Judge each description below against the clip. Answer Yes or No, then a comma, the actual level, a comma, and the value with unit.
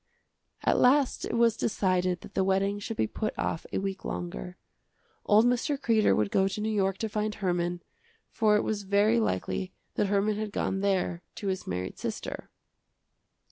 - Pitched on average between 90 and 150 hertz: No, high, 200 Hz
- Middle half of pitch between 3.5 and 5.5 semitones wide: No, average, 2.7 semitones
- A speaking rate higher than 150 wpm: Yes, average, 180 wpm